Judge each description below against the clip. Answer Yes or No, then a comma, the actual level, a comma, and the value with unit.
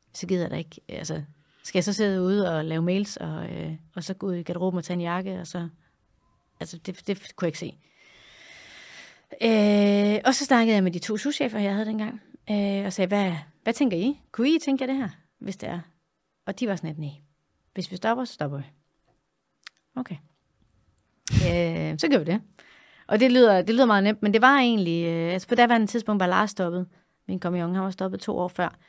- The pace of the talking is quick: Yes, fast, 225 wpm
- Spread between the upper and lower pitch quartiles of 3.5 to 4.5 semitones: Yes, average, 4.1 semitones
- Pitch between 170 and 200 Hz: Yes, high, 190 Hz